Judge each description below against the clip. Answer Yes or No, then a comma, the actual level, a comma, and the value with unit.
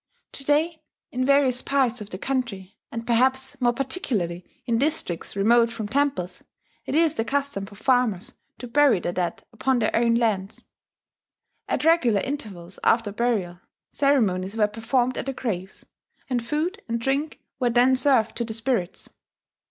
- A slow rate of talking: No, average, 160 wpm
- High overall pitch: Yes, high, 235 Hz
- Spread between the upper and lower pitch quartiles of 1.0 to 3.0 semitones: No, average, 4.5 semitones